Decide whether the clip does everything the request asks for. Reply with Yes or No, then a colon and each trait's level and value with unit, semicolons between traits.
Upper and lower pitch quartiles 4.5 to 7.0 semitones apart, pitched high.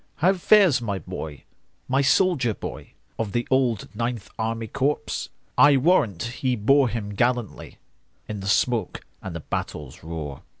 No: average, 4.8 semitones; low, 115 Hz